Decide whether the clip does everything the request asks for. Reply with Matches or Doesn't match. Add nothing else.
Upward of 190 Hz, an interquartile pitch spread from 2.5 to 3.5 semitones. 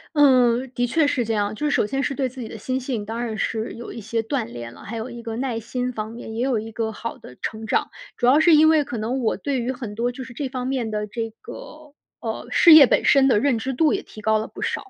Matches